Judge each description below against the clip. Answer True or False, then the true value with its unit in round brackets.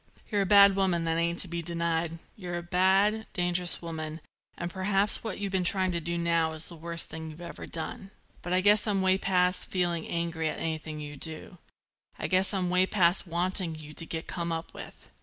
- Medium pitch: True (175 Hz)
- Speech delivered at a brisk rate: True (215 wpm)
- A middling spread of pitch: False (2.3 semitones)